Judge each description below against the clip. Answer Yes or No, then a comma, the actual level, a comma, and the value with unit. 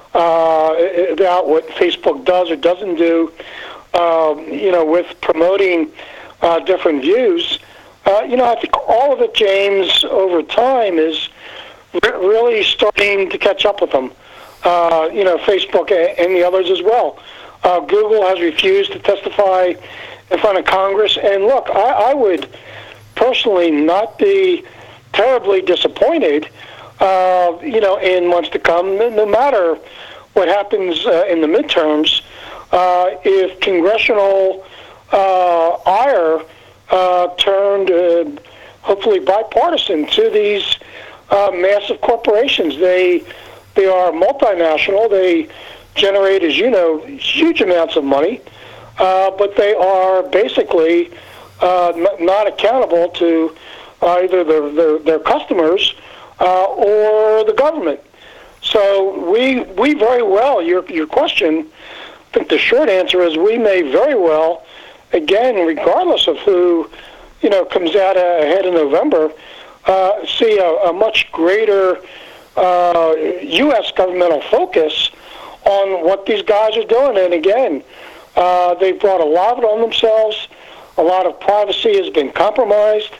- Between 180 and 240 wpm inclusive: No, slow, 135 wpm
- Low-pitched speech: No, high, 190 Hz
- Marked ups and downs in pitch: No, average, 4.6 semitones